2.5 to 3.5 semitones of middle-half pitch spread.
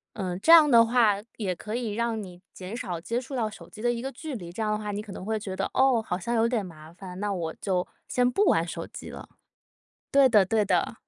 No: average, 4.4 semitones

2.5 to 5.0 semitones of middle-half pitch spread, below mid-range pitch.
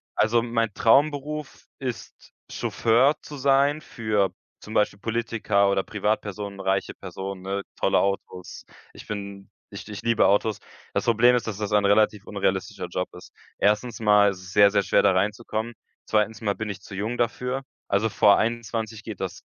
Yes: average, 2.8 semitones; low, 105 Hz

